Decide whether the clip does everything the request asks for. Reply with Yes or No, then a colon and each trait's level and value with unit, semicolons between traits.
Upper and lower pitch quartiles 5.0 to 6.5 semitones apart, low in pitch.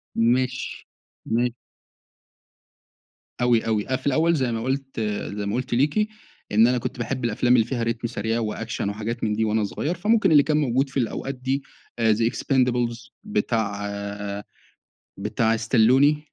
No: average, 3.1 semitones; low, 120 Hz